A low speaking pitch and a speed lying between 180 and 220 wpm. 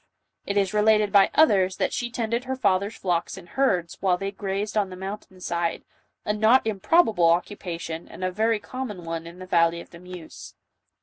No: high, 195 Hz; average, 190 wpm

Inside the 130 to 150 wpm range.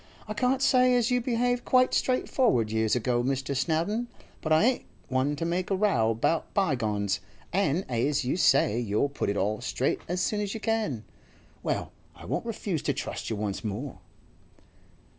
No: average, 180 wpm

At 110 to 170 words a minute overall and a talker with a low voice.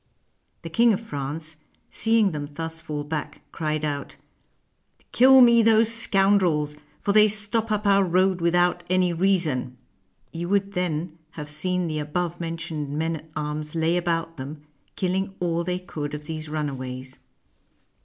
No: average, 155 wpm; medium, 165 Hz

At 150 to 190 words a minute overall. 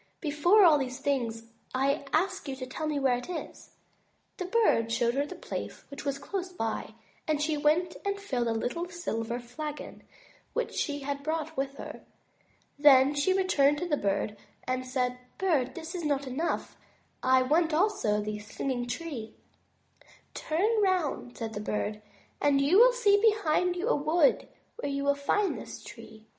Yes: average, 170 wpm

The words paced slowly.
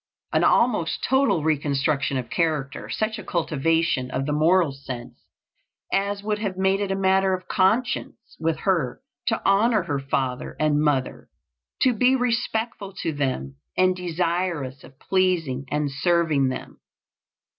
No: average, 145 wpm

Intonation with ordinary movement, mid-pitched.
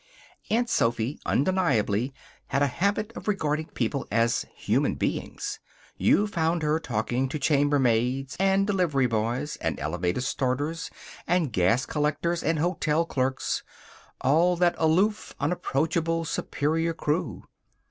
Yes: average, 4.8 semitones; medium, 150 Hz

